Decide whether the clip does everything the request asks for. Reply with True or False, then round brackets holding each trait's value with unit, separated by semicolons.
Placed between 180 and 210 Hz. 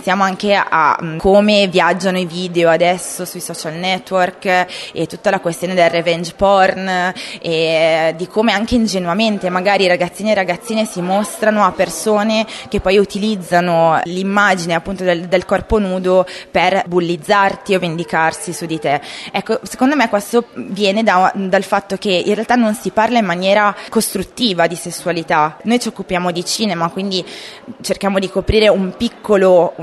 True (190 Hz)